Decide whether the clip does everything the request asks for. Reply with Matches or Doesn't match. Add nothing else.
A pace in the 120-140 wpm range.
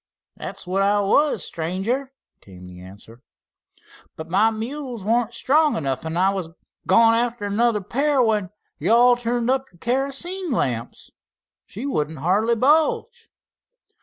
Matches